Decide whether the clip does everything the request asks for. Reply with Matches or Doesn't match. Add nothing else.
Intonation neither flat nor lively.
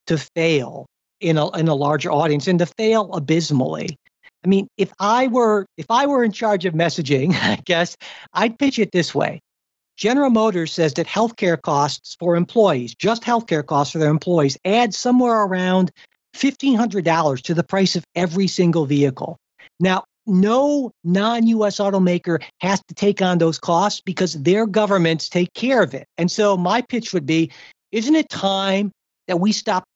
Matches